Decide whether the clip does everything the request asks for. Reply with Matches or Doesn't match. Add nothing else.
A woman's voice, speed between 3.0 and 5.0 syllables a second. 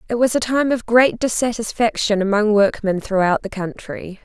Matches